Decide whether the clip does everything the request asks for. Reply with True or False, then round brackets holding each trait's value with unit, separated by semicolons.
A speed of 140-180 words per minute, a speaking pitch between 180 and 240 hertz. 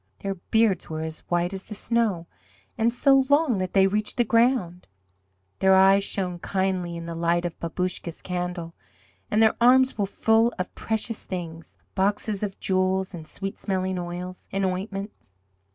True (165 wpm; 190 Hz)